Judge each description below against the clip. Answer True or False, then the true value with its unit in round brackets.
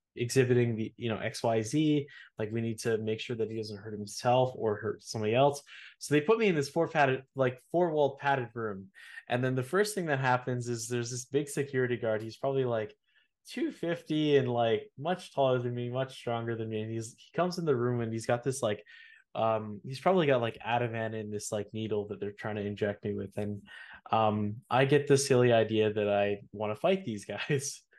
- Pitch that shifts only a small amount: False (4.1 semitones)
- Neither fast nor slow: False (220 wpm)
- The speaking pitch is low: True (120 Hz)